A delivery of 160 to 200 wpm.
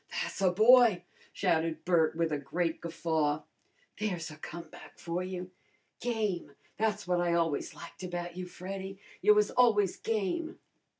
No: average, 145 wpm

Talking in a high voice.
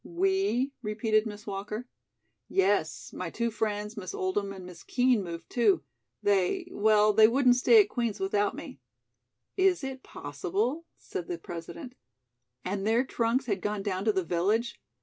Yes: high, 210 Hz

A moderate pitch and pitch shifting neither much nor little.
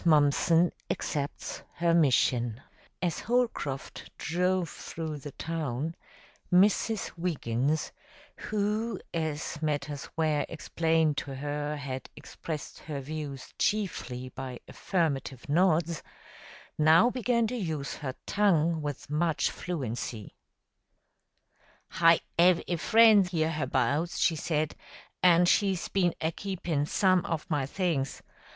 Yes: medium, 160 Hz; average, 3.7 semitones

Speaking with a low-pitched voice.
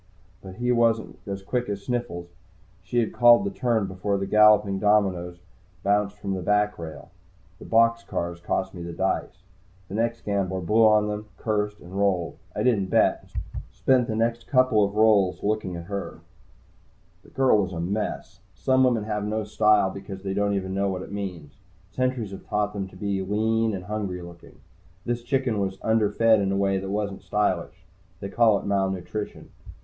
Yes: low, 100 Hz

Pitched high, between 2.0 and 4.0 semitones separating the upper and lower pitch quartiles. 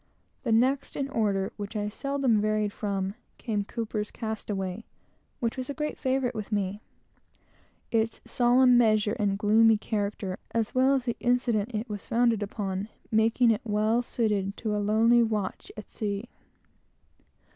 Yes: high, 220 Hz; narrow, 2.6 semitones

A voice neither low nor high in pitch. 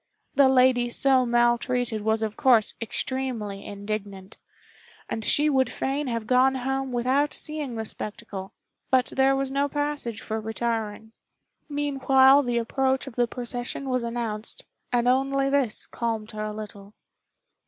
No: high, 245 Hz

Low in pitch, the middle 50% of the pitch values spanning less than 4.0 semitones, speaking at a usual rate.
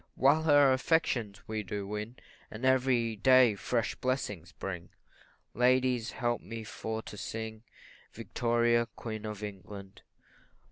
No: low, 115 Hz; average, 3.3 semitones; slow, 125 wpm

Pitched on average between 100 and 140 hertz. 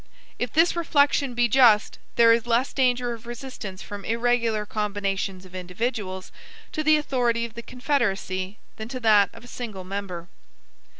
No: high, 230 Hz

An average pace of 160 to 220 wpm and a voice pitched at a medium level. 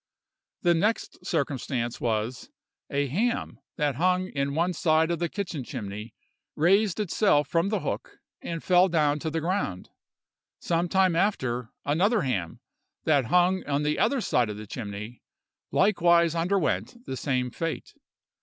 No: average, 145 wpm; medium, 160 Hz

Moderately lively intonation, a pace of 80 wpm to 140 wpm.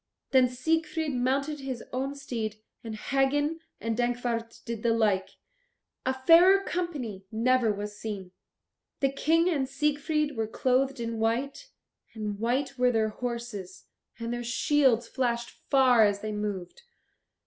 Yes: average, 3.8 semitones; slow, 135 wpm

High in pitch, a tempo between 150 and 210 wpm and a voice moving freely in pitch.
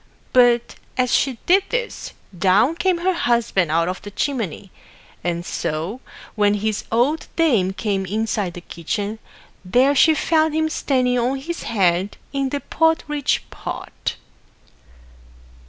No: high, 235 Hz; slow, 135 wpm; wide, 7.1 semitones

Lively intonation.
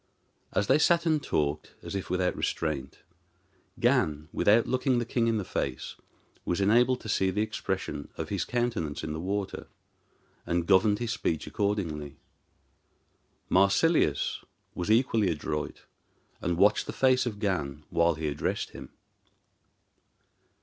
Yes: wide, 6.5 semitones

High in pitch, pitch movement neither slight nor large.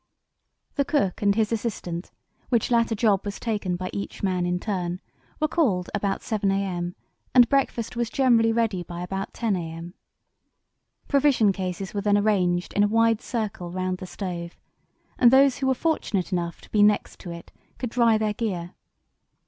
Yes: high, 205 Hz; average, 4.2 semitones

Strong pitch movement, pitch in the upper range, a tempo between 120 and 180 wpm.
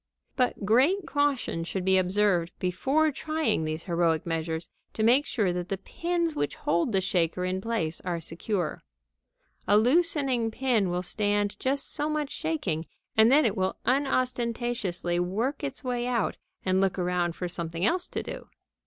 Yes: wide, 7.1 semitones; high, 205 Hz; average, 165 wpm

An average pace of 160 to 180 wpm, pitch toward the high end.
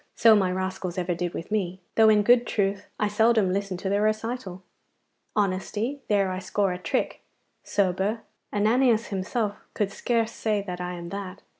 Yes: average, 170 wpm; high, 200 Hz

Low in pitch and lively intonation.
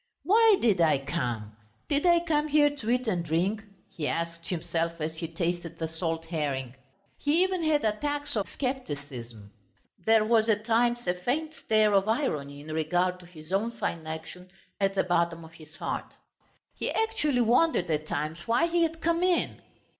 No: high, 190 Hz; wide, 8.6 semitones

